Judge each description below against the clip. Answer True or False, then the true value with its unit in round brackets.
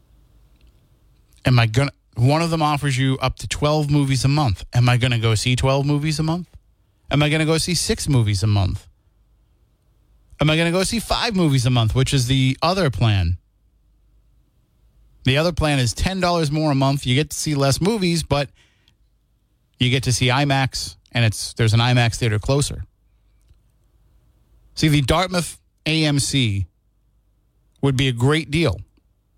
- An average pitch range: False (5.7 semitones)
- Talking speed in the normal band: True (165 wpm)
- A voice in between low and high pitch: False (130 Hz)